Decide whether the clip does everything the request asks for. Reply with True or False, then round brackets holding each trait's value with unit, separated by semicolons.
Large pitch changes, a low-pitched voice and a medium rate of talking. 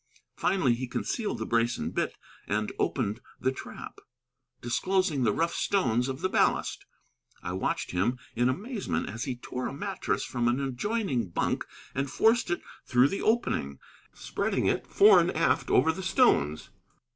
True (8.0 semitones; 130 Hz; 160 wpm)